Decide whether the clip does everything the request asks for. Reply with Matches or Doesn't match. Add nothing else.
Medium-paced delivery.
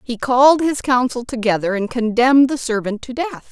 Matches